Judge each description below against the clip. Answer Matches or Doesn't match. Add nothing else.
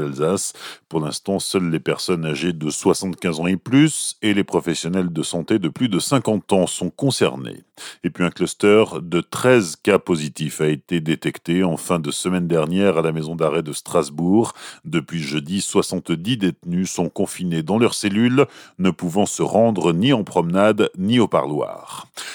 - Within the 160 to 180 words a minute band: Matches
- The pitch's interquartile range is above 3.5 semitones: Doesn't match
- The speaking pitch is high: Doesn't match